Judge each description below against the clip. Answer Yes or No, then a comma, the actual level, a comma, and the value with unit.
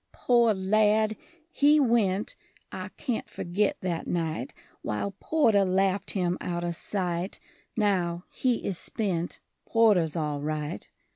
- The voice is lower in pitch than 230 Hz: Yes, high, 190 Hz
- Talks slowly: Yes, slow, 120 wpm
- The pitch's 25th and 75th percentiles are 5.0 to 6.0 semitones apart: No, average, 4.0 semitones